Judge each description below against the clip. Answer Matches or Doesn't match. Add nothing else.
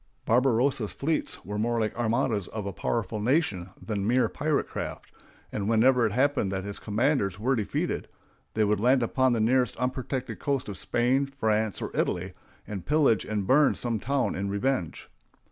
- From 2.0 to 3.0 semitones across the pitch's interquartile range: Doesn't match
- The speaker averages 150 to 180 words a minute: Matches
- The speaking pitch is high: Doesn't match